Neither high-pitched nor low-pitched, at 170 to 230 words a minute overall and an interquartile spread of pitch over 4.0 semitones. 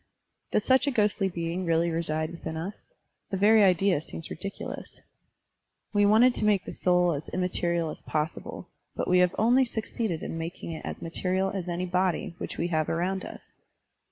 No: medium, 180 Hz; average, 180 wpm; average, 3.2 semitones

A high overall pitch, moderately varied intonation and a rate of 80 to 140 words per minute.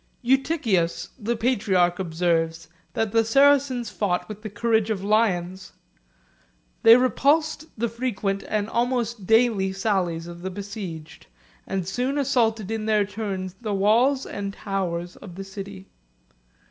Yes: high, 205 Hz; average, 3.8 semitones; slow, 135 wpm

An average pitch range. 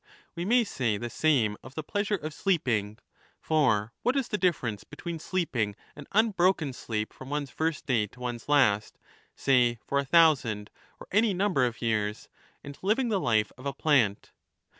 No: wide, 7.1 semitones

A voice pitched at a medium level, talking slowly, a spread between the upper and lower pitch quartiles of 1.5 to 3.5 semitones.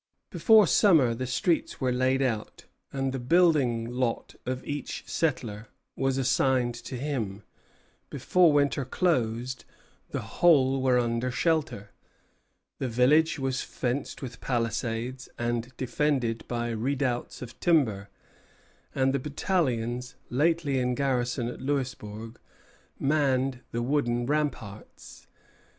No: low, 130 Hz; slow, 120 wpm; average, 3.0 semitones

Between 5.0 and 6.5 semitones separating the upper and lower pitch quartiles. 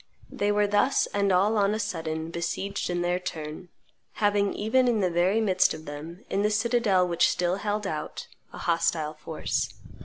No: average, 3.6 semitones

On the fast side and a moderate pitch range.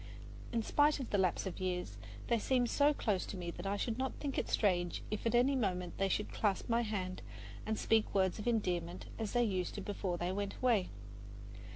Yes: fast, 215 wpm; average, 4.3 semitones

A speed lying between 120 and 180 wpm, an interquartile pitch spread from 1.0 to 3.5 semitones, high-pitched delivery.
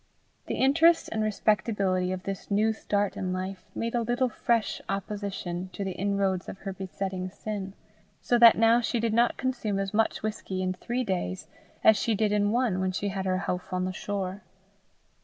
No: average, 190 wpm; average, 2.9 semitones; high, 200 Hz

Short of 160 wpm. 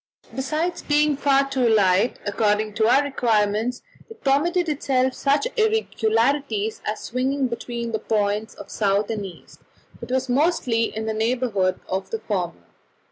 Yes: average, 145 wpm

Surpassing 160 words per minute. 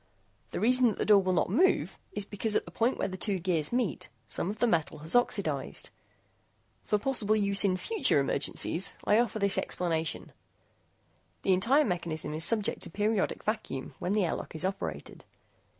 Yes: average, 180 wpm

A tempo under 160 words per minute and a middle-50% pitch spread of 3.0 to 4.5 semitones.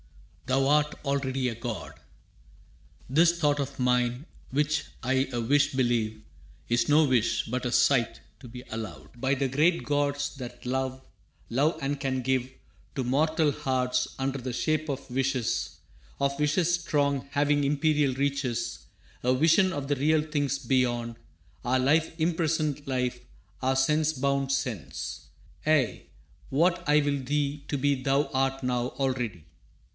No: average, 145 wpm; narrow, 2.5 semitones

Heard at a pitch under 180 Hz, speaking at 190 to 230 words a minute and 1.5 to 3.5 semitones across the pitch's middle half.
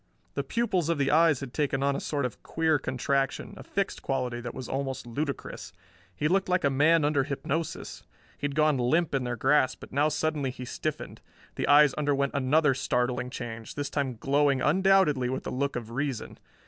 Yes: medium, 140 Hz; average, 195 wpm; average, 2.9 semitones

